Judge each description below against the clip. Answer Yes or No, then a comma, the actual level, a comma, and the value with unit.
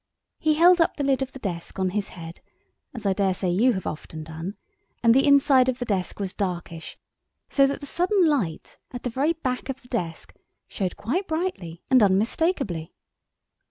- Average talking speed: Yes, average, 190 wpm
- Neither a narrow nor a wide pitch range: No, wide, 7.2 semitones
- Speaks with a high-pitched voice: Yes, high, 235 Hz